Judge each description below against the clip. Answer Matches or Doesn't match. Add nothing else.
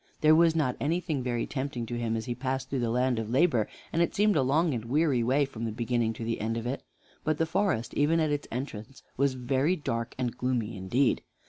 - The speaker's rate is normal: Doesn't match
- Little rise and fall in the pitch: Doesn't match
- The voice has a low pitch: Matches